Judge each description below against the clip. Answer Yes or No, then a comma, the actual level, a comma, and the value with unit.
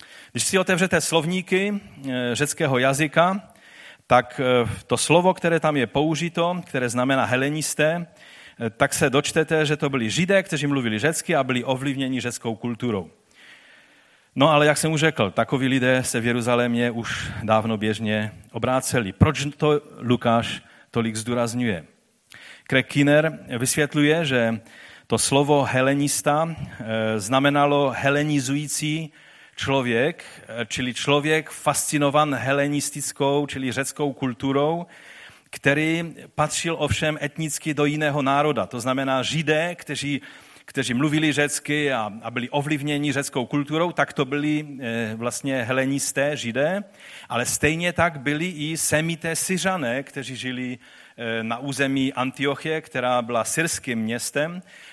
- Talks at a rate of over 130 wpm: No, average, 120 wpm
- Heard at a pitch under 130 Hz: No, medium, 140 Hz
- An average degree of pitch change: Yes, average, 3.5 semitones